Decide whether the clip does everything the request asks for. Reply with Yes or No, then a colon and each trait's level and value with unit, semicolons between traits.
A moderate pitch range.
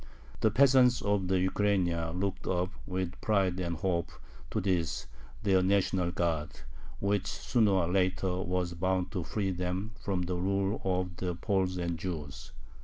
No: narrow, 1.8 semitones